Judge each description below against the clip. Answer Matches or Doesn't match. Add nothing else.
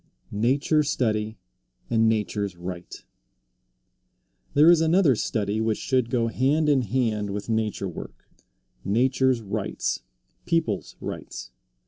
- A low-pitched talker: Matches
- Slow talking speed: Matches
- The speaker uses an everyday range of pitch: Matches